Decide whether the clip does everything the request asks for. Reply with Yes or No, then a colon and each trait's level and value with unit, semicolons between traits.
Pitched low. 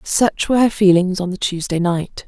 No: high, 190 Hz